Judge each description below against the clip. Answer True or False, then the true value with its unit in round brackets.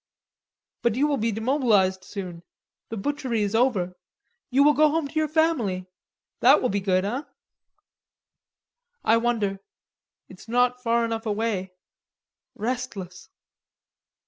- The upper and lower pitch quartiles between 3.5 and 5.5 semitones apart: True (4.9 semitones)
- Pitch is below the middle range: False (230 Hz)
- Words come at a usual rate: False (125 wpm)